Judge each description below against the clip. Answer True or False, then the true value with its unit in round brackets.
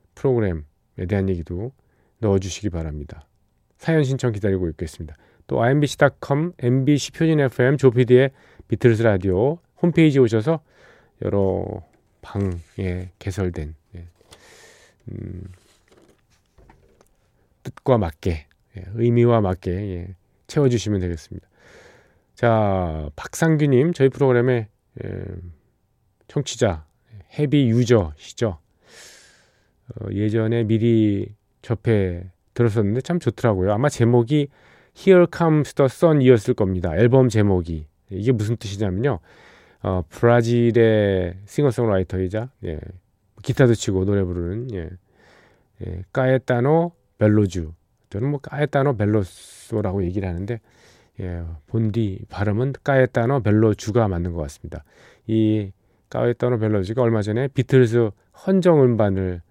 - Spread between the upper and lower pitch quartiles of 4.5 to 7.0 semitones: True (5.1 semitones)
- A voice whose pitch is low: True (110 Hz)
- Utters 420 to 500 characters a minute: False (265 characters per minute)